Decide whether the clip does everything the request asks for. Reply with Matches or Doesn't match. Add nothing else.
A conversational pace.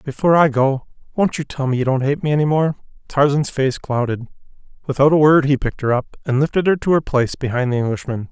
Doesn't match